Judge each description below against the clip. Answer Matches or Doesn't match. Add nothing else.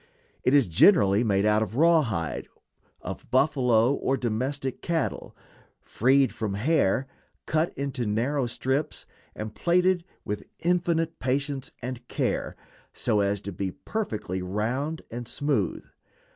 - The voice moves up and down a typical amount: Doesn't match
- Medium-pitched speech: Doesn't match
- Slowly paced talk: Matches